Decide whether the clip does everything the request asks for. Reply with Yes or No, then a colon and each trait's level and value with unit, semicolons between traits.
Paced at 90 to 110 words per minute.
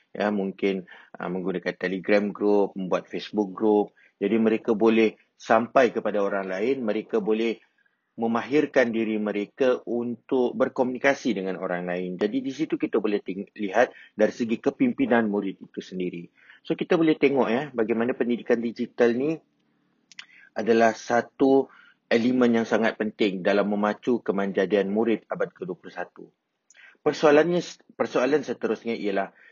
No: average, 130 wpm